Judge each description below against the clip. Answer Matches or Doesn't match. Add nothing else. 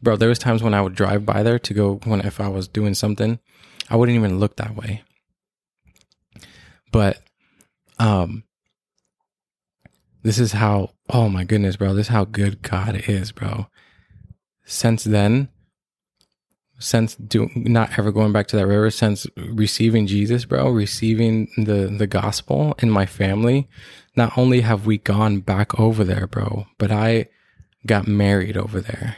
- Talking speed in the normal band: Matches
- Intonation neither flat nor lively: Doesn't match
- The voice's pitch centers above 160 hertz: Doesn't match